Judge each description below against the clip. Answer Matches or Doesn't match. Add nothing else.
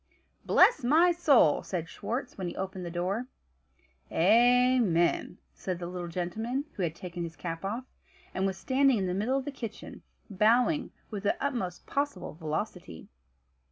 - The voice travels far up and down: Matches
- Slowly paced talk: Doesn't match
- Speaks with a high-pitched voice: Matches